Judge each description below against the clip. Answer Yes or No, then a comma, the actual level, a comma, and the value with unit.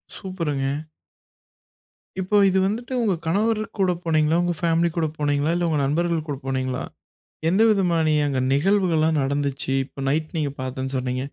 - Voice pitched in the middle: Yes, medium, 160 Hz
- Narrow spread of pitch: No, average, 4.4 semitones